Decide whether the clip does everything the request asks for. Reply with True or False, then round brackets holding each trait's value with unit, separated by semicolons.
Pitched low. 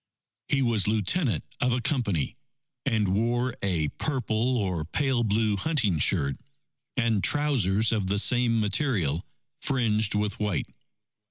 True (110 Hz)